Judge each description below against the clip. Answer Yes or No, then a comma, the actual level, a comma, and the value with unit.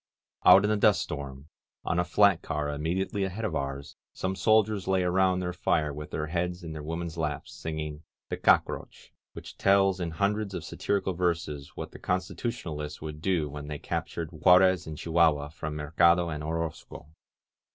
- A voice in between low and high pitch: No, very low, 85 Hz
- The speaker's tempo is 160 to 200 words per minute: Yes, average, 185 wpm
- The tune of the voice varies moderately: Yes, average, 3.6 semitones